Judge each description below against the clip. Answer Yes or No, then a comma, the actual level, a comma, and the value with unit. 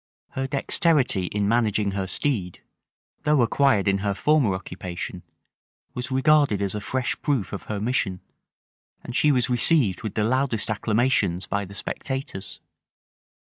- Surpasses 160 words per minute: No, average, 140 wpm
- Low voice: Yes, low, 110 Hz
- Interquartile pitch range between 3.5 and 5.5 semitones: Yes, average, 5.1 semitones